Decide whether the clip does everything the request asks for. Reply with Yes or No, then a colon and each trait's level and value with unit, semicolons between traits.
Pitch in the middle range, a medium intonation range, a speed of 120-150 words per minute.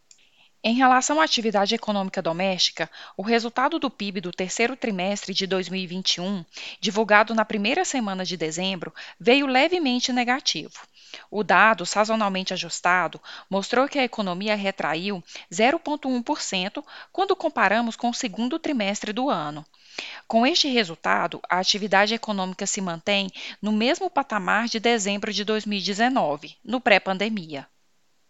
No: high, 215 Hz; average, 4.3 semitones; average, 125 wpm